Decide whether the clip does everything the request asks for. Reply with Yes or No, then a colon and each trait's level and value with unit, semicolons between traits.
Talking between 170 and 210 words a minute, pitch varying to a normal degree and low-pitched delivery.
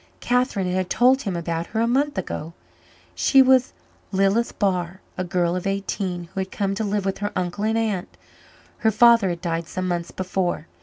No: average, 190 wpm; average, 3.8 semitones; high, 195 Hz